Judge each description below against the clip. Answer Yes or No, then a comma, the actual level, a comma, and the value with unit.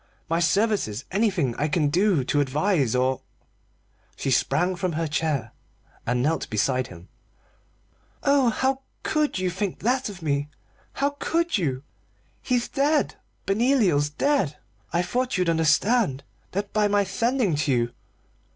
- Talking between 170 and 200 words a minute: No, average, 140 wpm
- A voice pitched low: No, medium, 180 Hz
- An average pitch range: No, wide, 7.9 semitones